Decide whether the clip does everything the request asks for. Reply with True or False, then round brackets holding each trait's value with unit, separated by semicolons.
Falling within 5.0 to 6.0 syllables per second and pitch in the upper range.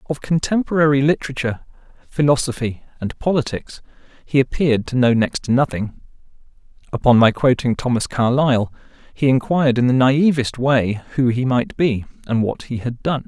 False (5.4 syllables/s; 130 Hz)